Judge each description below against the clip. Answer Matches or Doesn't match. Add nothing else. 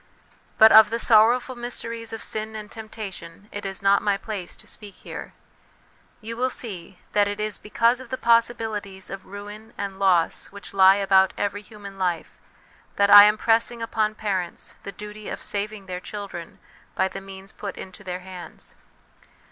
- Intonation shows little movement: Matches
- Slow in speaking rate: Doesn't match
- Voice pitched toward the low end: Doesn't match